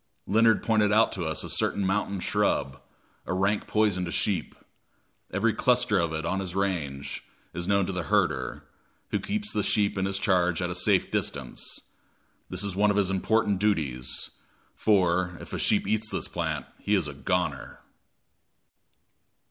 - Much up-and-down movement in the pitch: No, average, 3.1 semitones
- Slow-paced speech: No, average, 170 wpm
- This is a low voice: Yes, very low, 95 Hz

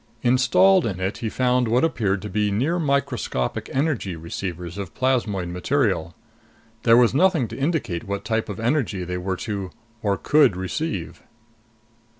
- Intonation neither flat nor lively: No, wide, 5.9 semitones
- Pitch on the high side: No, low, 110 Hz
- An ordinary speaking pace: Yes, average, 155 wpm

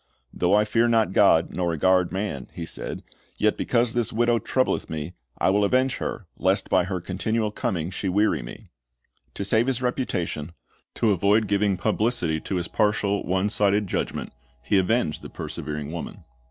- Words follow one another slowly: No, average, 170 wpm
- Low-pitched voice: Yes, low, 100 Hz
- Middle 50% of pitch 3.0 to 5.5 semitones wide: Yes, average, 3.9 semitones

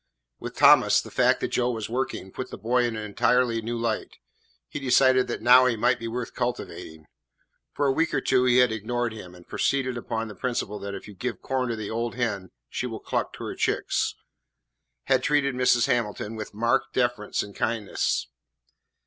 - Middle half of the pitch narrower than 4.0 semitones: Yes, narrow, 2.6 semitones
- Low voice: Yes, low, 120 Hz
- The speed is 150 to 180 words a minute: No, average, 200 wpm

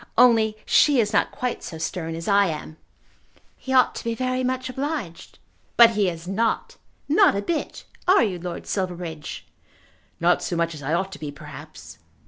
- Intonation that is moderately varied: No, wide, 7.1 semitones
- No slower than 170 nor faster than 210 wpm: Yes, average, 180 wpm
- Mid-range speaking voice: No, high, 195 Hz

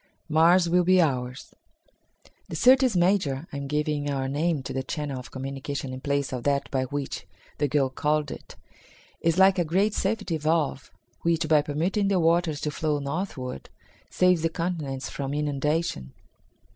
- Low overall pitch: No, medium, 150 Hz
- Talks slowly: No, average, 165 wpm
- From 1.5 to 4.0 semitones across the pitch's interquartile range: Yes, average, 3.7 semitones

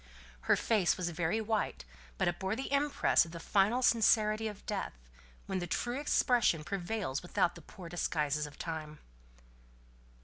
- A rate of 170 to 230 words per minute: No, average, 160 wpm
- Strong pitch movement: No, average, 5.0 semitones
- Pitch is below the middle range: No, high, 190 Hz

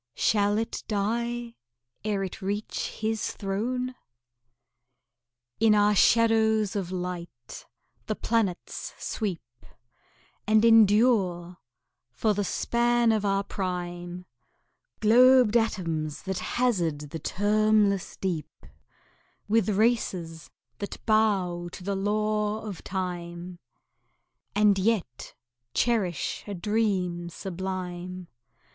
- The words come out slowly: Yes, slow, 95 wpm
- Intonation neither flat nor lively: Yes, average, 3.5 semitones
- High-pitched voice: Yes, high, 200 Hz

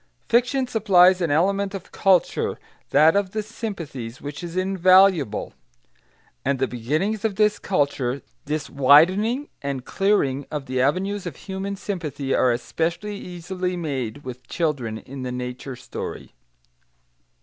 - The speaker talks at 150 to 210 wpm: No, slow, 135 wpm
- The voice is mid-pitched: Yes, medium, 170 Hz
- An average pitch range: No, wide, 6.4 semitones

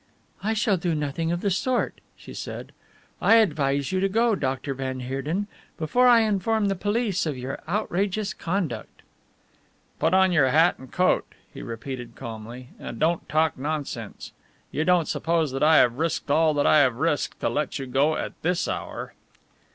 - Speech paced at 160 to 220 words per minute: Yes, average, 175 wpm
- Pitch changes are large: Yes, wide, 5.9 semitones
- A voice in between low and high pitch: Yes, medium, 160 Hz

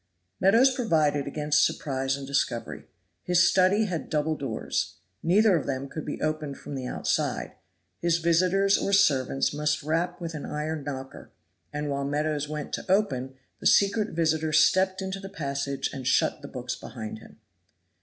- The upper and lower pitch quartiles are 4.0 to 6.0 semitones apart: Yes, average, 4.7 semitones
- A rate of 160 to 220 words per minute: Yes, average, 165 wpm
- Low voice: No, medium, 155 Hz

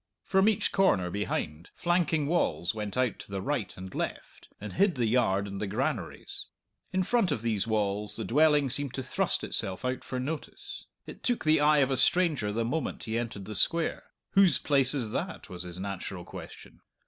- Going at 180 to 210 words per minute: Yes, average, 195 wpm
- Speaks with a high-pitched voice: No, low, 125 Hz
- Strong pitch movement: Yes, wide, 7.2 semitones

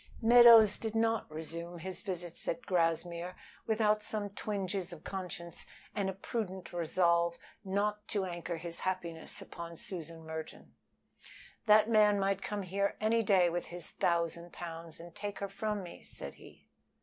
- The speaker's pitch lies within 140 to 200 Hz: Yes, medium, 185 Hz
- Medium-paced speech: Yes, average, 150 wpm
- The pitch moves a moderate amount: Yes, average, 3.4 semitones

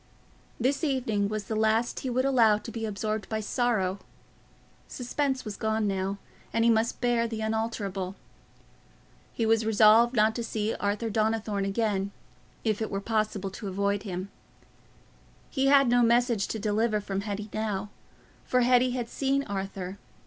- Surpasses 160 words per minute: No, average, 155 wpm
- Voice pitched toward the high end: Yes, high, 220 Hz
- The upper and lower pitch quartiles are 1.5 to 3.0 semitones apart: Yes, narrow, 2.6 semitones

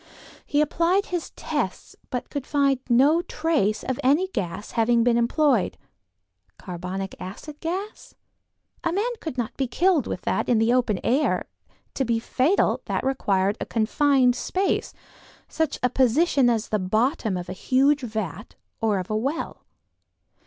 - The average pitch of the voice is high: Yes, very high, 255 Hz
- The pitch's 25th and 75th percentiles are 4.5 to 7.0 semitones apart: Yes, wide, 5.6 semitones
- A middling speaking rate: Yes, average, 150 wpm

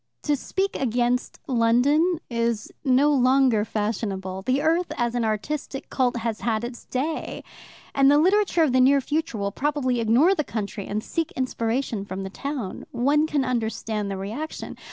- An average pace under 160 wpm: No, average, 165 wpm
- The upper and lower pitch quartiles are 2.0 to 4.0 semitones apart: No, average, 4.7 semitones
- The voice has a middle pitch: No, very high, 250 Hz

